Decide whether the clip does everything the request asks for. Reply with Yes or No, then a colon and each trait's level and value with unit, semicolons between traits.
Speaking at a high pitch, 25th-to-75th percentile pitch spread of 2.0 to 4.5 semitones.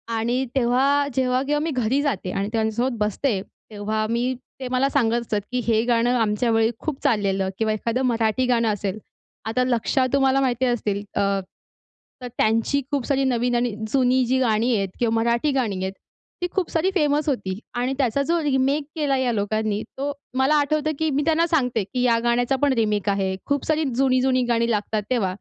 Yes: high, 245 Hz; average, 3.5 semitones